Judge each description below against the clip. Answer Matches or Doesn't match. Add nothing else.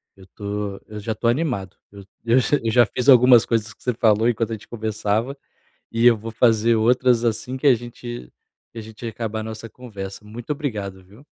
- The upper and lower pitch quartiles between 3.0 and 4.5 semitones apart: Doesn't match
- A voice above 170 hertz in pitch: Doesn't match